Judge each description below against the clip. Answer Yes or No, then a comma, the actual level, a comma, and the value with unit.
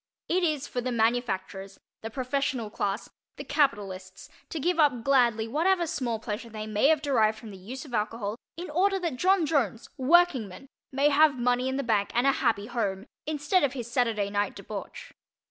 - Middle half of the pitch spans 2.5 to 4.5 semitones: No, average, 5.2 semitones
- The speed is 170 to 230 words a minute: Yes, average, 185 wpm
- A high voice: Yes, high, 245 Hz